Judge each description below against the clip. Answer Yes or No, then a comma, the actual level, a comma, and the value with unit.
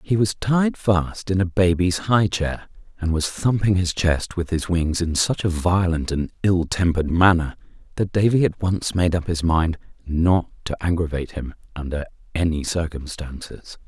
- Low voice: Yes, very low, 90 Hz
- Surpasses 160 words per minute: Yes, average, 175 wpm